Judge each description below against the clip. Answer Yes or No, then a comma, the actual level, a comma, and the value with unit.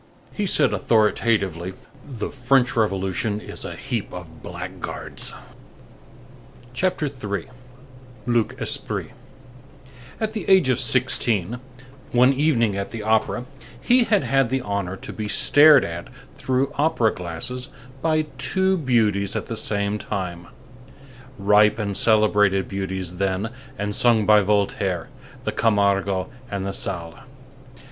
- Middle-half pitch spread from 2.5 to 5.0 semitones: Yes, average, 4.6 semitones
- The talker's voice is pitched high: No, low, 110 Hz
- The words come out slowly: Yes, slow, 120 wpm